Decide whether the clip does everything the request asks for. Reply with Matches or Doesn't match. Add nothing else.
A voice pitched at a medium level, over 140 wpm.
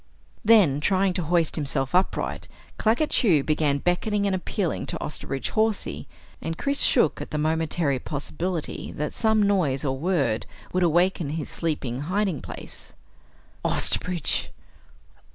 Doesn't match